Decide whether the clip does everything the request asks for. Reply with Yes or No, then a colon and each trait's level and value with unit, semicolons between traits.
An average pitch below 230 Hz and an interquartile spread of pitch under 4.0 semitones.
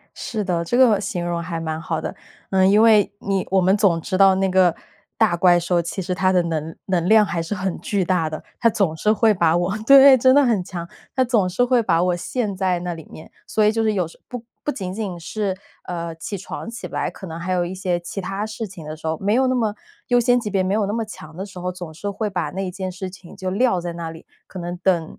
Yes: high, 190 Hz; average, 3.4 semitones